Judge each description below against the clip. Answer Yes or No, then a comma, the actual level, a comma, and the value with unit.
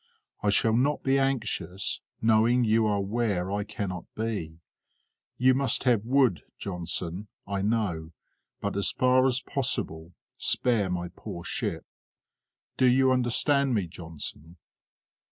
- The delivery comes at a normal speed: No, slow, 130 wpm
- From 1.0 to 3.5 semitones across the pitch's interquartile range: No, wide, 5.5 semitones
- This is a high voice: No, low, 110 Hz